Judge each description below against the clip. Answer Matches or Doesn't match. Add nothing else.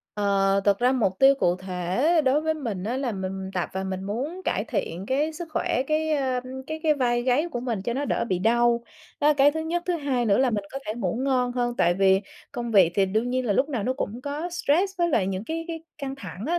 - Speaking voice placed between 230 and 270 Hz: Matches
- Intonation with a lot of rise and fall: Matches